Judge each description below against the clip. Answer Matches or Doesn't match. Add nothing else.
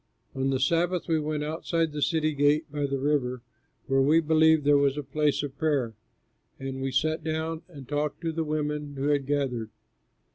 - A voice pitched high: Doesn't match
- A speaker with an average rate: Matches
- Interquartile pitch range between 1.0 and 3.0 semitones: Matches